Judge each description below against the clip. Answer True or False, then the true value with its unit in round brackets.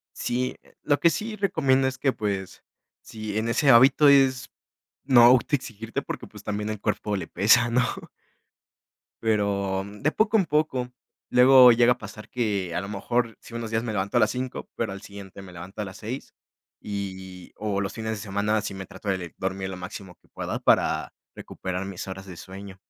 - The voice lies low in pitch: True (110 Hz)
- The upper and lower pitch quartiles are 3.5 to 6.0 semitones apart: True (4.2 semitones)